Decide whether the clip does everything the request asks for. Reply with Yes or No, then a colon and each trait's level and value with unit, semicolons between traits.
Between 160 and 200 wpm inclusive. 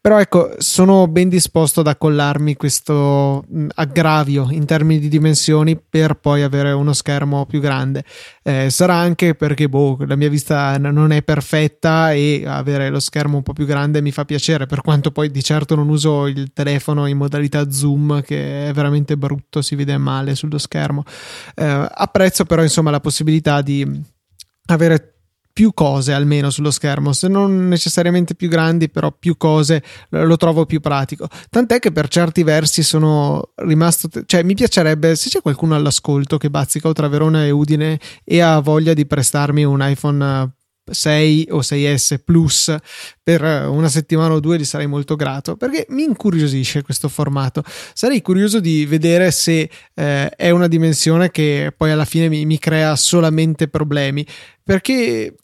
Yes: average, 165 wpm